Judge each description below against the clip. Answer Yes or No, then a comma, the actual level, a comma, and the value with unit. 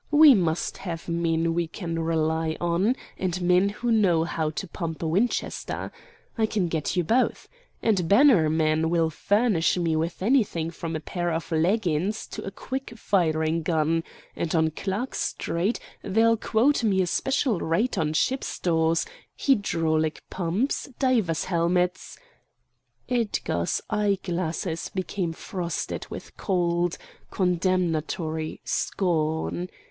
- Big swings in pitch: No, average, 3.9 semitones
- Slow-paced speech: Yes, slow, 130 wpm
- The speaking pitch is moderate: Yes, medium, 175 Hz